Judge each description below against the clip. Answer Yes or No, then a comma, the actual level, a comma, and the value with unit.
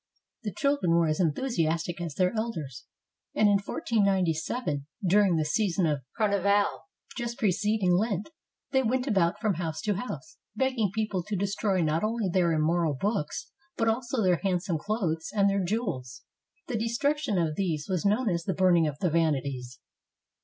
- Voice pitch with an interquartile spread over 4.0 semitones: Yes, average, 4.9 semitones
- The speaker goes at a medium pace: Yes, average, 165 wpm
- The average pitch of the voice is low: No, high, 190 Hz